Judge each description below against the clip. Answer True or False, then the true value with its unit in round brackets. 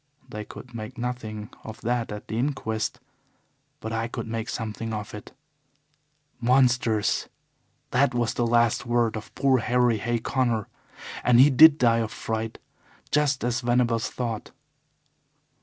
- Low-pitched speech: True (115 Hz)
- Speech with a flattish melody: True (2.0 semitones)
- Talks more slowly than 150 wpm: True (140 wpm)